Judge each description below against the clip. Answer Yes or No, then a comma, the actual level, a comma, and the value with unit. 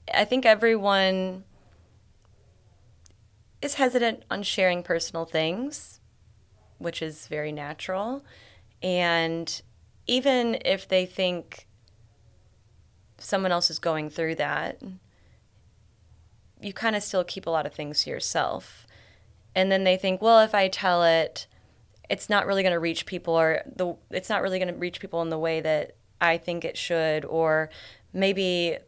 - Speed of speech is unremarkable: Yes, average, 145 wpm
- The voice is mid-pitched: Yes, medium, 165 Hz